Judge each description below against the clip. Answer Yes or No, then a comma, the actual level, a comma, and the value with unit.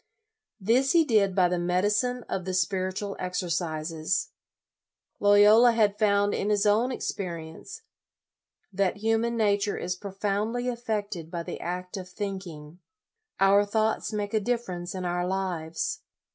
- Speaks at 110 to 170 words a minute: Yes, slow, 135 wpm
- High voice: Yes, high, 200 Hz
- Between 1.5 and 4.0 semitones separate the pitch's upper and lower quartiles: Yes, average, 3.1 semitones